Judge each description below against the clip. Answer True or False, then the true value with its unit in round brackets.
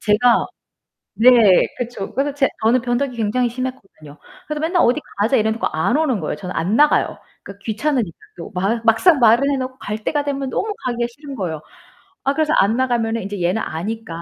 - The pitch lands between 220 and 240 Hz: True (235 Hz)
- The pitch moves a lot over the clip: False (4.7 semitones)